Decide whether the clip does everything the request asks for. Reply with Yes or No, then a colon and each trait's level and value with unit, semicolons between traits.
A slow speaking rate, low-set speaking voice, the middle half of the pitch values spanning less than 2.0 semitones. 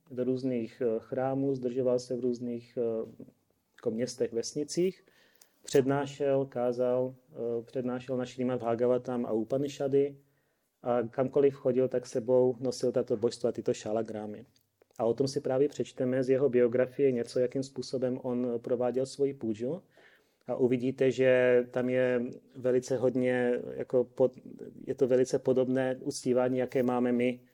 No: average, 130 wpm; low, 125 Hz; narrow, 1.3 semitones